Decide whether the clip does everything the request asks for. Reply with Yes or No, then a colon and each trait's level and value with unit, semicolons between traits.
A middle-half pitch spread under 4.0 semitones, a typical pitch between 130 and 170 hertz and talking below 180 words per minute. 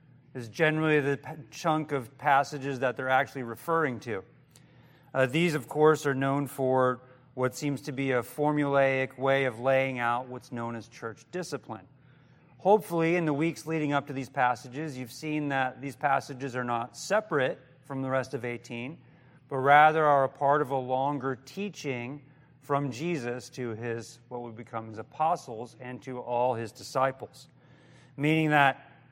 Yes: average, 2.8 semitones; low, 135 Hz; average, 165 wpm